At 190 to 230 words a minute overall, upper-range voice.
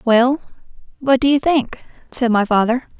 No: average, 160 wpm; very high, 250 Hz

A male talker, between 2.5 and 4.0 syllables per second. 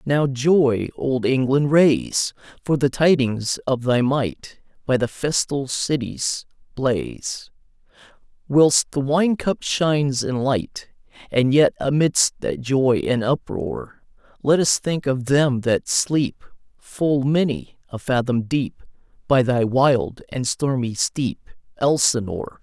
Yes: male; 3.5 syllables/s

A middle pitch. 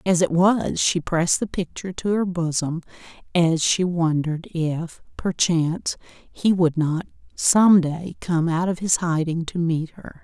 Yes: medium, 170 Hz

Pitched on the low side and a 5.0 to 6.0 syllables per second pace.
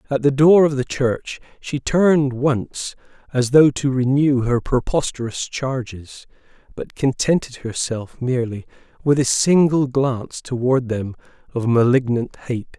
No: low, 130 Hz; 4.2 syllables/s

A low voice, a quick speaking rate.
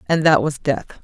No: medium, 150 Hz; fast, 235 wpm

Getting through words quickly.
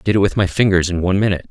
Yes: fast, 360 wpm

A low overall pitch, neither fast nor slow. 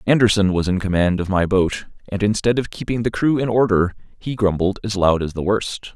No: low, 100 Hz; fast, 220 wpm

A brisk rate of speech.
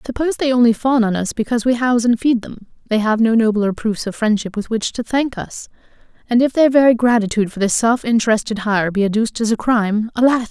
Yes: fast, 230 wpm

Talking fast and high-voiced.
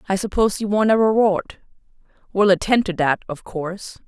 No: average, 160 wpm; high, 195 Hz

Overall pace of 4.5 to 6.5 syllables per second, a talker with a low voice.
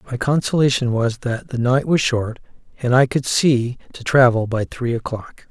Yes: 4.6 syllables/s; low, 125 Hz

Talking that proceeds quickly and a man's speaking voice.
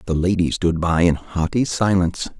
No: average, 175 wpm; male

